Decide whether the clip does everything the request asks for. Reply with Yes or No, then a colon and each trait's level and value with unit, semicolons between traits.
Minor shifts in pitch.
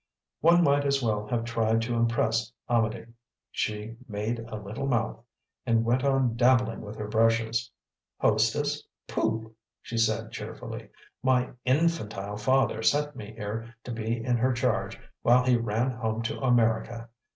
Yes: narrow, 2.2 semitones